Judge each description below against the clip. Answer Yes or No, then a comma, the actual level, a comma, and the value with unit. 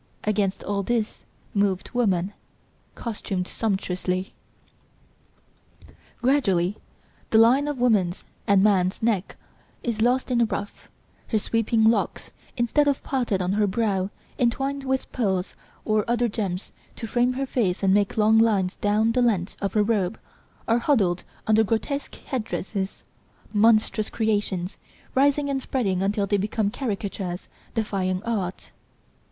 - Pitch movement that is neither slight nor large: Yes, average, 3.5 semitones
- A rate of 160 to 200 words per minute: No, slow, 135 wpm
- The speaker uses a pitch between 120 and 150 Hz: No, high, 215 Hz